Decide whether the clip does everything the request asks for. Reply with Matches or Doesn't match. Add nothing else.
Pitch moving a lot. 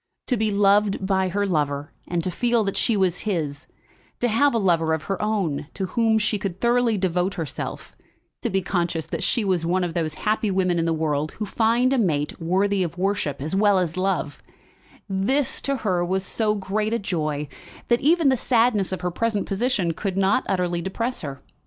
Doesn't match